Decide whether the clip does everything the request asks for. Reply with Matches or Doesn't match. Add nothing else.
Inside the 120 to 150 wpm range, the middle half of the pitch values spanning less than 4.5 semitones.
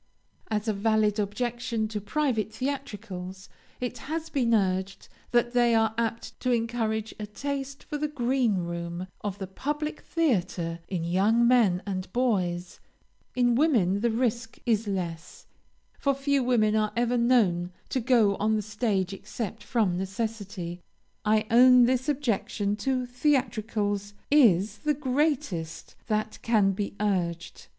Matches